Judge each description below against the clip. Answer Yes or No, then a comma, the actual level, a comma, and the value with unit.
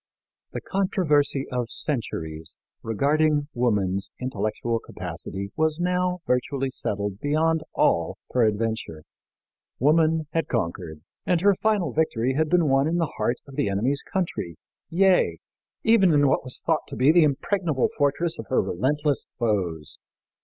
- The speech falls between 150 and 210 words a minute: No, average, 140 wpm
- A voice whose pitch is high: No, medium, 140 Hz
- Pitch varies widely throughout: Yes, wide, 6.8 semitones